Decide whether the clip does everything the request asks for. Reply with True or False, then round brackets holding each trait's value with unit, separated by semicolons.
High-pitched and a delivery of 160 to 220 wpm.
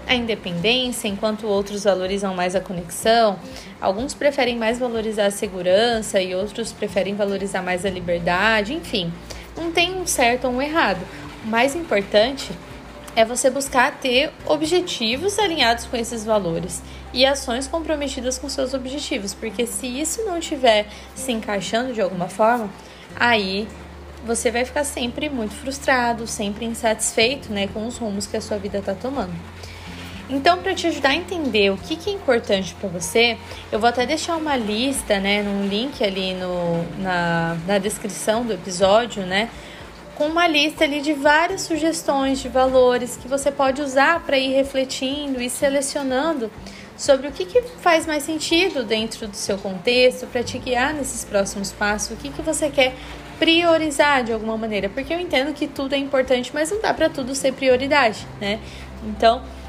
True (245 Hz; 165 wpm)